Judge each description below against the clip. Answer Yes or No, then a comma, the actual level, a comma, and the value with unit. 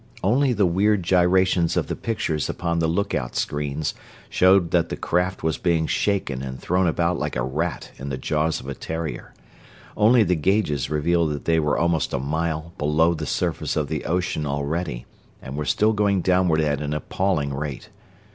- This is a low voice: Yes, very low, 80 Hz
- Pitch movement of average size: Yes, average, 3.6 semitones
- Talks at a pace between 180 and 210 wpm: Yes, average, 185 wpm